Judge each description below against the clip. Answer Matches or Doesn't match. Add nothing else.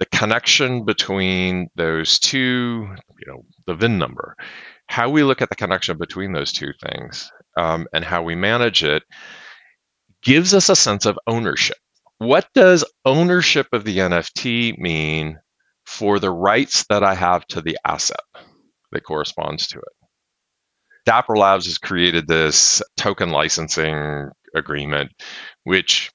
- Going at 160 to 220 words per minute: Doesn't match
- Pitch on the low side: Matches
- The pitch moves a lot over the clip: Matches